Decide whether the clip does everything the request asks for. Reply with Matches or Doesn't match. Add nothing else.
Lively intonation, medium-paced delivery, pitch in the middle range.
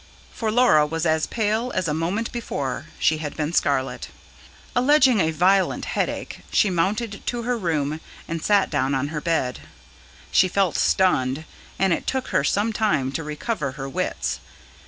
Matches